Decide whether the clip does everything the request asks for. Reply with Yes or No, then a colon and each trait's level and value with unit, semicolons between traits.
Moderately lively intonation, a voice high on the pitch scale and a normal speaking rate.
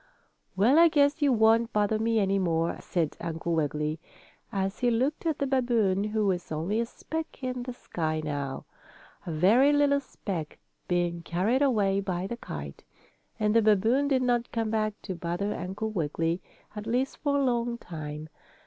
No: wide, 6.1 semitones; high, 210 Hz; average, 175 wpm